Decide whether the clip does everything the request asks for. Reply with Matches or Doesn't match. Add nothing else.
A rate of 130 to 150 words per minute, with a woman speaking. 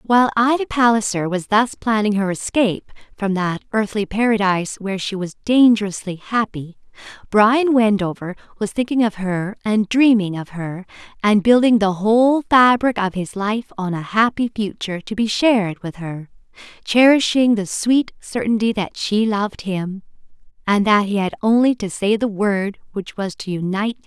Doesn't match